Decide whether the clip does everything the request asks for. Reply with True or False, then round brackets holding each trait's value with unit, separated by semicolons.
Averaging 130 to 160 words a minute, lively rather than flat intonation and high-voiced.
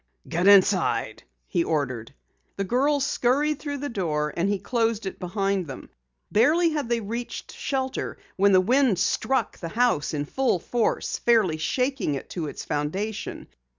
True (155 wpm; 6.8 semitones; 205 Hz)